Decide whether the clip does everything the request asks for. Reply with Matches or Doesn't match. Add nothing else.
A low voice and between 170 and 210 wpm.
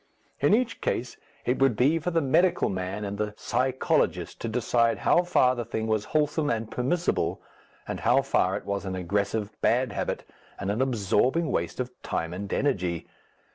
Matches